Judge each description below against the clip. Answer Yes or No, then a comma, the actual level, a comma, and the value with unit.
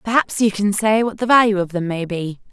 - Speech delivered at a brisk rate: Yes, fast, 260 wpm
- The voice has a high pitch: Yes, high, 205 Hz